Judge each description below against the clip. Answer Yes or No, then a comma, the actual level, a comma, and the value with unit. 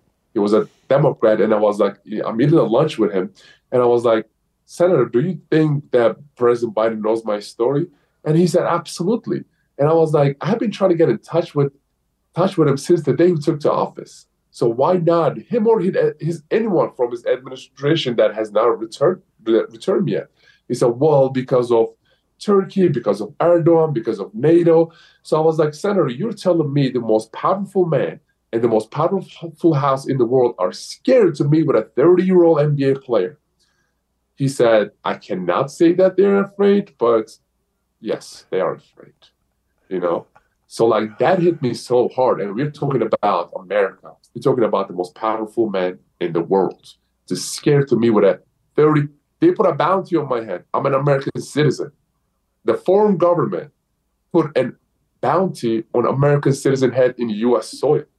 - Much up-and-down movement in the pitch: Yes, wide, 5.7 semitones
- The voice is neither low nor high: Yes, medium, 155 Hz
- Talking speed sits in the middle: Yes, average, 185 wpm